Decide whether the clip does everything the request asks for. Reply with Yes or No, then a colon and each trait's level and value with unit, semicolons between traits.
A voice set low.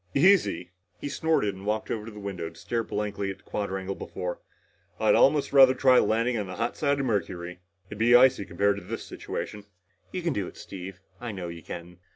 Yes: low, 105 Hz